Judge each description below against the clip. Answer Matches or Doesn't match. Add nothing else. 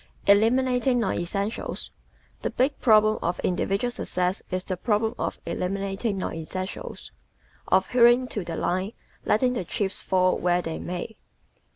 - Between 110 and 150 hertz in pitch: Doesn't match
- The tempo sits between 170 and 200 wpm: Doesn't match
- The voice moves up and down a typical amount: Matches